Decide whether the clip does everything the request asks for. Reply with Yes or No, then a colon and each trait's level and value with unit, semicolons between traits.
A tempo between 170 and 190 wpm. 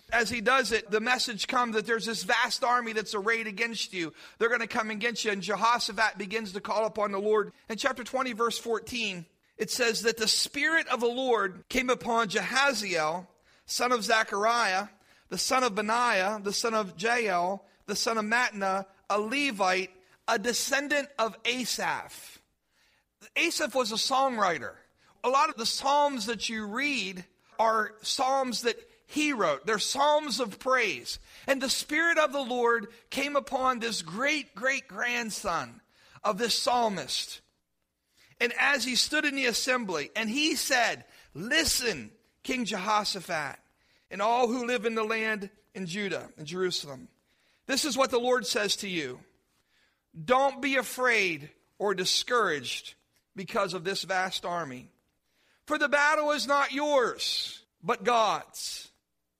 No: average, 155 wpm